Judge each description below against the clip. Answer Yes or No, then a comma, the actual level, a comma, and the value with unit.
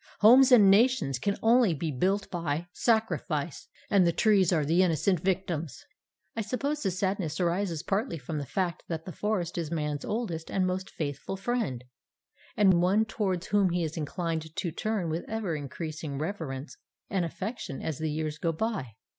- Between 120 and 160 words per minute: No, average, 175 wpm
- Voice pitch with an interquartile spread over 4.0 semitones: Yes, average, 4.4 semitones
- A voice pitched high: No, medium, 175 Hz